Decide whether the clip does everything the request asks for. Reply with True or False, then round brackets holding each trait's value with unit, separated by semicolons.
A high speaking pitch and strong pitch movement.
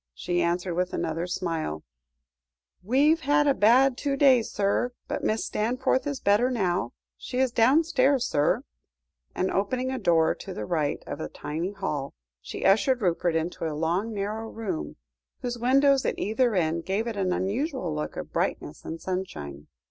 True (200 Hz; 7.0 semitones)